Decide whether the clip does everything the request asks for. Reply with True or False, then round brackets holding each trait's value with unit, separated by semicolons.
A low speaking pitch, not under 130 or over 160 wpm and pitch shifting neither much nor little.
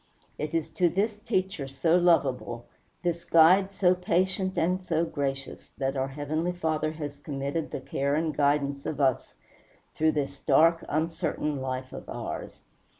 False (155 Hz; 150 wpm; 3.8 semitones)